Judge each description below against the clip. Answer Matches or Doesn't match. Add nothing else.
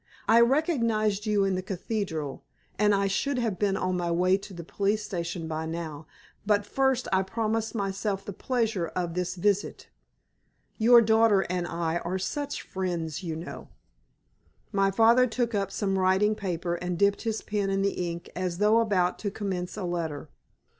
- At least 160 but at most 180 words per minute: Matches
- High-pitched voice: Matches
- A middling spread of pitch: Matches